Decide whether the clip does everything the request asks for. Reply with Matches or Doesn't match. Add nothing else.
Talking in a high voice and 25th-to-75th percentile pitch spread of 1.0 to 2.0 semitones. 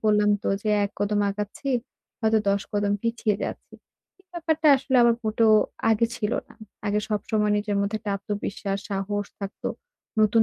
Matches